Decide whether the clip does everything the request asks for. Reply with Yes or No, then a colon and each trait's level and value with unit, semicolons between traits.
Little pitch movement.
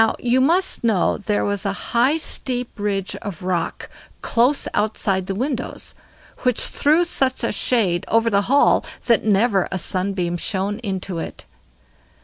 No: average, 4.3 semitones